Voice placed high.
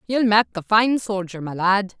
Yes: high, 205 Hz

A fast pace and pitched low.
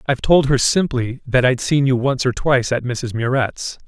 Yes: fast, 215 wpm; low, 130 Hz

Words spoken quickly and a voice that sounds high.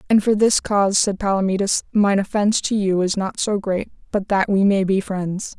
Yes: fast, 215 wpm; high, 200 Hz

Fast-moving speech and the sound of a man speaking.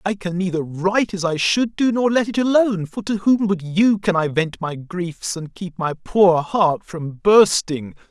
Yes: fast, 215 wpm; male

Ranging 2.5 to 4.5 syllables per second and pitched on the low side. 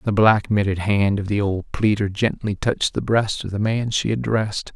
No: 5.0 syllables/s; low, 105 Hz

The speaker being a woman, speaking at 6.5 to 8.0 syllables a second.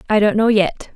No: female; 5.2 syllables/s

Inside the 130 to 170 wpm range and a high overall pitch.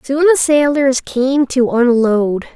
Yes: average, 140 wpm; very high, 260 Hz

